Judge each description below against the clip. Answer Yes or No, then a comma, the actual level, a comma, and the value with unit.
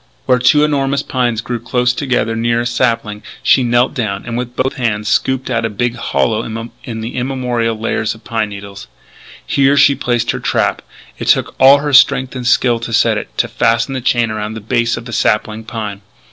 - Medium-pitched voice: No, low, 120 Hz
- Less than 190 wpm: No, average, 200 wpm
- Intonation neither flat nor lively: No, narrow, 2.2 semitones